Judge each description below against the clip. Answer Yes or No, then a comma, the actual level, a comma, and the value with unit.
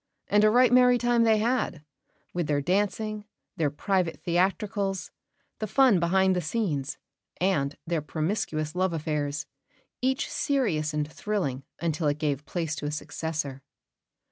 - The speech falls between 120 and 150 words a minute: Yes, average, 140 wpm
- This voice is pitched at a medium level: Yes, medium, 175 Hz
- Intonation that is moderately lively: No, wide, 5.7 semitones